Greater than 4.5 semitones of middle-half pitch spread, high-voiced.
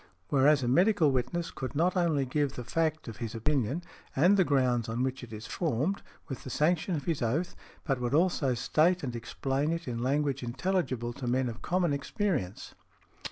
No: average, 5.2 semitones; medium, 140 Hz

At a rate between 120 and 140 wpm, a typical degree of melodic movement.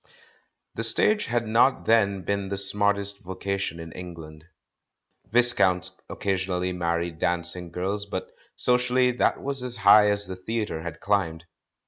Yes: slow, 135 wpm; average, 3.6 semitones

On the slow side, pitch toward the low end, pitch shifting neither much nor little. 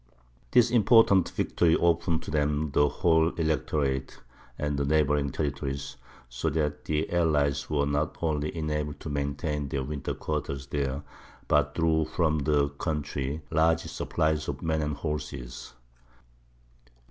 No: slow, 130 wpm; very low, 75 Hz; narrow, 2.0 semitones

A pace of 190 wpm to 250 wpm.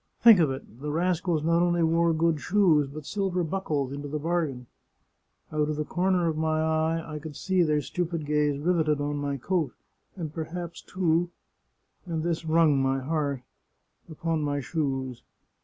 No: average, 175 wpm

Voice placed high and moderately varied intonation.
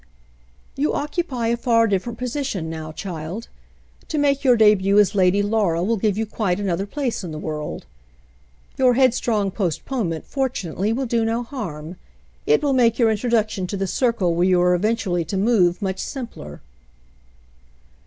Yes: high, 210 Hz; average, 4.9 semitones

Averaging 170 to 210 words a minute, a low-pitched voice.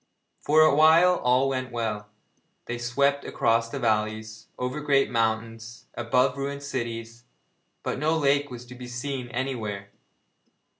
No: slow, 135 wpm; low, 125 Hz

